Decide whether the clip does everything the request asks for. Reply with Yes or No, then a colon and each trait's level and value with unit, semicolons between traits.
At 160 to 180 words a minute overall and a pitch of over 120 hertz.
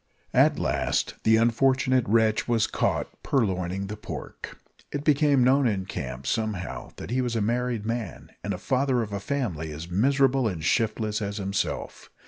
No: average, 165 wpm; low, 110 Hz